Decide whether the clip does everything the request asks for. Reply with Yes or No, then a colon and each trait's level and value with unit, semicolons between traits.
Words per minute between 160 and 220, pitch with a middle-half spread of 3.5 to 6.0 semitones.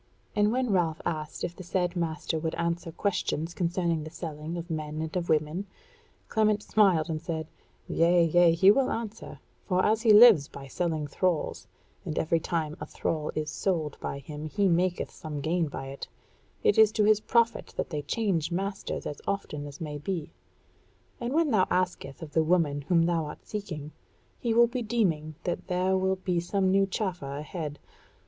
Yes: average, 185 wpm; average, 4.0 semitones